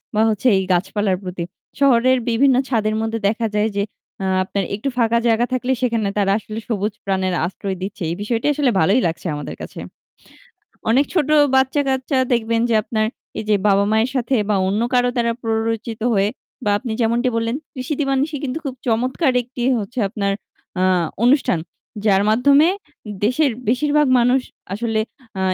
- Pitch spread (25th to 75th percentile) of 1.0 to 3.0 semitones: No, average, 3.7 semitones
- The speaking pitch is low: No, high, 230 Hz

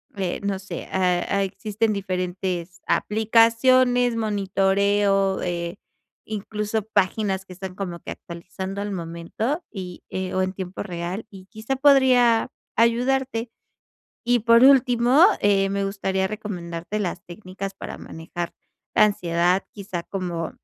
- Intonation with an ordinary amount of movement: Yes, average, 3.5 semitones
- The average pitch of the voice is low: No, high, 195 Hz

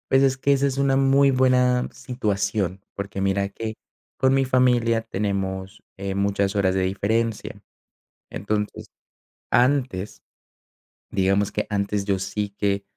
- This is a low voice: Yes, low, 105 Hz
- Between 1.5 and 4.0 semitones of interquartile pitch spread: No, average, 4.4 semitones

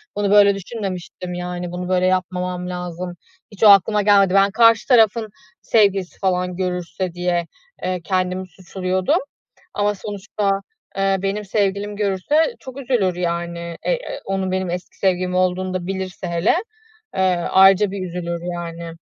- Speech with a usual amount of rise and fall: No, narrow, 2.0 semitones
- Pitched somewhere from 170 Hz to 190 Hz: Yes, medium, 185 Hz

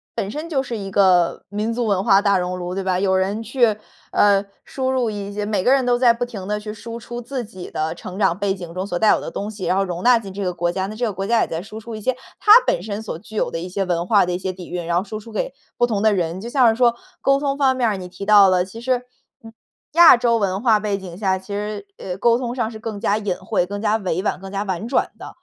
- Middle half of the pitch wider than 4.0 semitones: No, average, 3.6 semitones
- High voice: Yes, high, 205 Hz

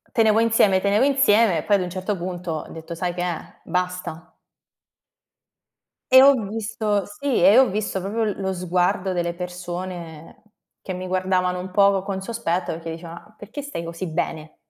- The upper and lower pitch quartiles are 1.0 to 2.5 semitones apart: No, average, 2.9 semitones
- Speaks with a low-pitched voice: No, medium, 185 Hz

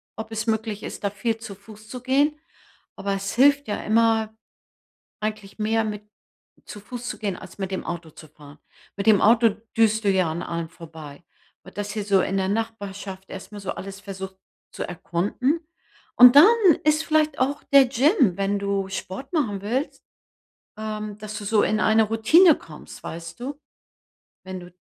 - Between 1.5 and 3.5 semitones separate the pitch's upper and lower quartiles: Yes, average, 2.9 semitones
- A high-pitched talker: Yes, high, 210 Hz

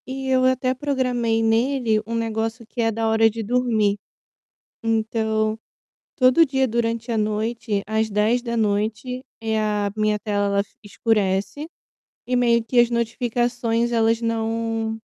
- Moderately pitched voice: No, high, 225 Hz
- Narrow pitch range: Yes, narrow, 1.8 semitones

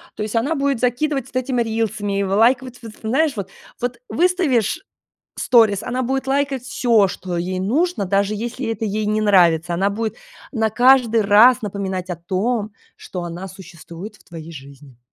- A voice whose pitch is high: Yes, high, 215 Hz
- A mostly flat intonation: No, average, 4.7 semitones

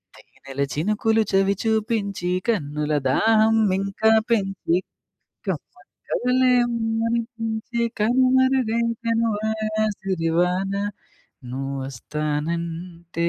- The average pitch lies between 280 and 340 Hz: No, high, 210 Hz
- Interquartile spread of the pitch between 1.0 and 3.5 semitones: No, average, 5.1 semitones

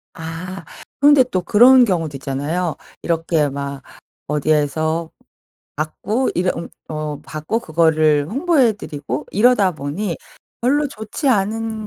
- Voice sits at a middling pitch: Yes, medium, 170 Hz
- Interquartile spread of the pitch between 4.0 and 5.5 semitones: No, wide, 6.4 semitones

